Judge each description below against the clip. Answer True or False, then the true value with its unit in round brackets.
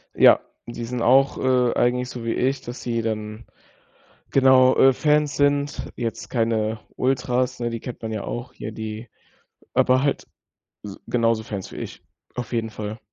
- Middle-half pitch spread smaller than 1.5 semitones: False (2.4 semitones)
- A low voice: True (120 Hz)